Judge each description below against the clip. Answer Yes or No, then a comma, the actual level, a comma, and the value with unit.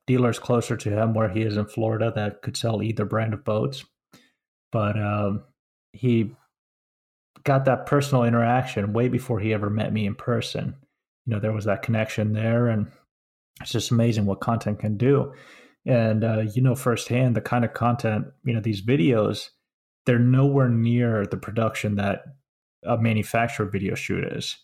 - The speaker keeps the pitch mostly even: Yes, narrow, 2.3 semitones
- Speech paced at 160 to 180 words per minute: Yes, average, 170 wpm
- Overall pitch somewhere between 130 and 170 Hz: No, low, 115 Hz